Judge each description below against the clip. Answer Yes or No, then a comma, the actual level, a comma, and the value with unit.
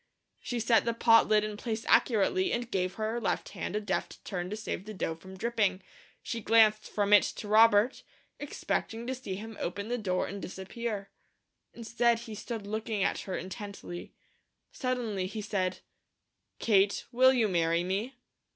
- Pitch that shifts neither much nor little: Yes, average, 3.0 semitones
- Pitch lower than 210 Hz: No, high, 215 Hz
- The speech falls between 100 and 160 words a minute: No, average, 170 wpm